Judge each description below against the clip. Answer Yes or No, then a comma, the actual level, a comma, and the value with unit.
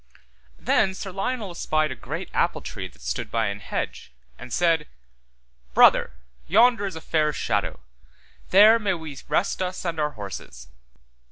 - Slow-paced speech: No, average, 155 wpm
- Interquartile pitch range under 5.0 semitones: No, wide, 5.6 semitones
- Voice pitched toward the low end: No, medium, 165 Hz